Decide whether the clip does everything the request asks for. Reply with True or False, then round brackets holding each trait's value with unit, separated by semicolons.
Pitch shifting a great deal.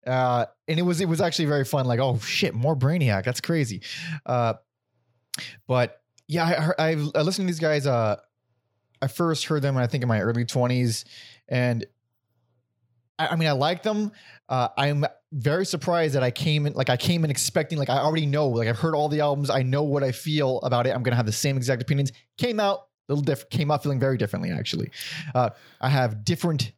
False (4.1 semitones)